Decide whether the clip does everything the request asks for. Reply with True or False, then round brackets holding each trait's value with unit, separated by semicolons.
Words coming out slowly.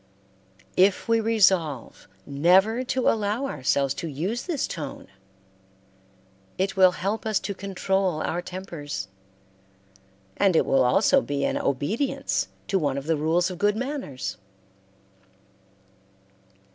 True (120 wpm)